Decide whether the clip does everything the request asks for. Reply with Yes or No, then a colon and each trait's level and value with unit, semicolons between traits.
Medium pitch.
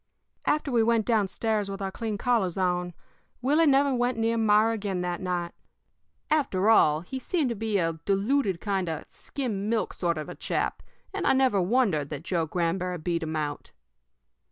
No: high, 200 Hz